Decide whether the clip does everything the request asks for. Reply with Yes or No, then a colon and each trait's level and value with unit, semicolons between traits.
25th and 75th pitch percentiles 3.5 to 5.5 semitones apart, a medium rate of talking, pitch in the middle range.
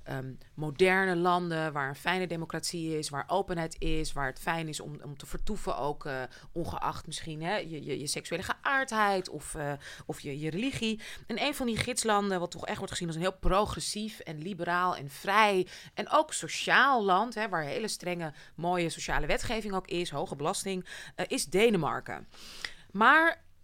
Yes: average, 4.4 semitones; average, 185 wpm; medium, 175 Hz